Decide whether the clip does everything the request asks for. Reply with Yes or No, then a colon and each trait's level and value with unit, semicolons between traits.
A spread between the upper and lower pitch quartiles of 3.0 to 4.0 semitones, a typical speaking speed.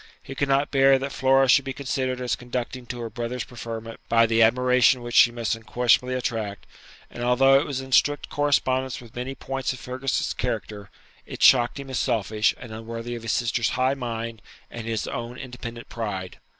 No: narrow, 2.4 semitones; average, 190 wpm